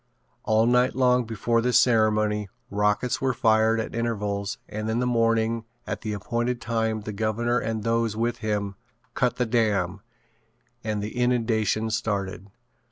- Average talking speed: Yes, average, 150 wpm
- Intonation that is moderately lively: No, narrow, 1.9 semitones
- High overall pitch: No, low, 110 Hz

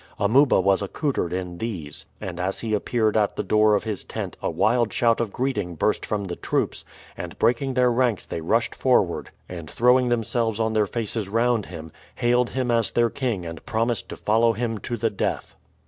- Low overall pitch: Yes, low, 110 Hz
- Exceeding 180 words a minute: Yes, average, 195 wpm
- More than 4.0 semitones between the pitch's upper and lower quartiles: No, average, 3.4 semitones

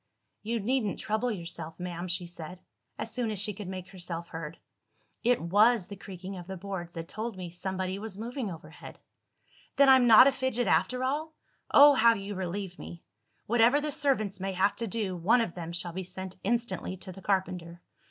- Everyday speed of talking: Yes, average, 190 wpm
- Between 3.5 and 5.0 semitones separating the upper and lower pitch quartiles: Yes, average, 4.6 semitones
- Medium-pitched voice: No, high, 195 Hz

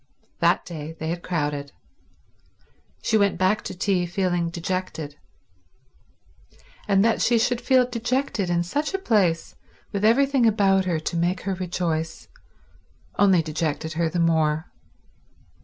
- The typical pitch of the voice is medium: Yes, medium, 180 Hz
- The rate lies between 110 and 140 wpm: Yes, slow, 135 wpm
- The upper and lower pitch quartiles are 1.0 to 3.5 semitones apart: No, average, 4.5 semitones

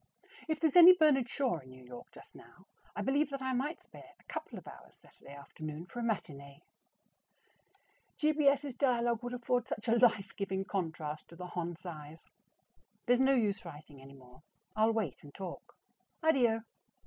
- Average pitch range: No, wide, 9.0 semitones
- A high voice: Yes, high, 215 Hz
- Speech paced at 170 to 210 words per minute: Yes, average, 180 wpm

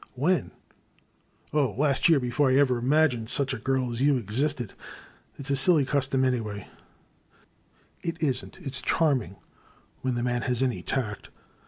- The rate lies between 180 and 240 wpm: Yes, average, 190 wpm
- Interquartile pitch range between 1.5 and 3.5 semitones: Yes, average, 2.7 semitones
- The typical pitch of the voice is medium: No, low, 130 Hz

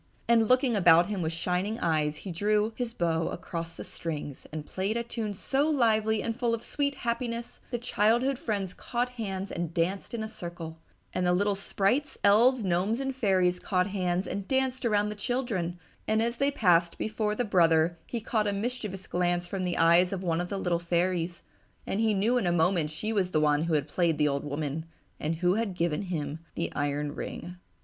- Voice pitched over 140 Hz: Yes, high, 190 Hz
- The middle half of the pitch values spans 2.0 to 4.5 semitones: No, average, 4.9 semitones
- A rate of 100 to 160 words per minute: No, fast, 205 wpm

